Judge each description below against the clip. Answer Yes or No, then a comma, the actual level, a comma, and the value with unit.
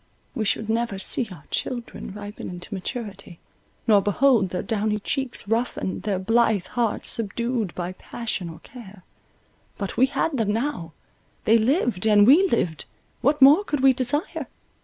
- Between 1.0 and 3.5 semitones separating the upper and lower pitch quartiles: No, average, 4.2 semitones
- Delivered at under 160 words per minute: Yes, average, 145 wpm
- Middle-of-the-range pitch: No, high, 220 Hz